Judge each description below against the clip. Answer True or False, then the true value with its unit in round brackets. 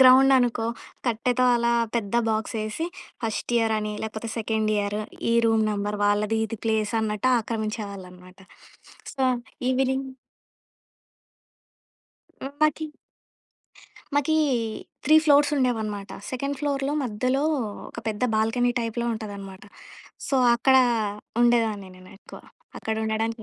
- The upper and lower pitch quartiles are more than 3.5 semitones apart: False (3.2 semitones)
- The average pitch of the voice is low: False (225 Hz)